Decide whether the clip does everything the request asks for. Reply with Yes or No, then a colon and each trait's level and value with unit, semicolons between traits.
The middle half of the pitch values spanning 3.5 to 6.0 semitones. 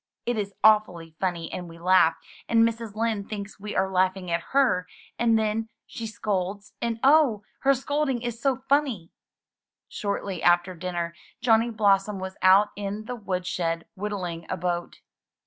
Yes: average, 3.9 semitones